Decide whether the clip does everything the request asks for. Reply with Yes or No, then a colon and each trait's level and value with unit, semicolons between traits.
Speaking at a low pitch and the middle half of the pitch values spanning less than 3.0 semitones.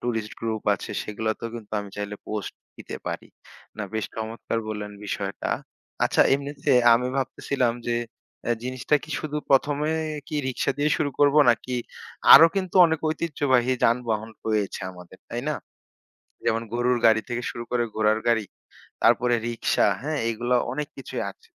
No: low, 120 Hz; average, 3.8 semitones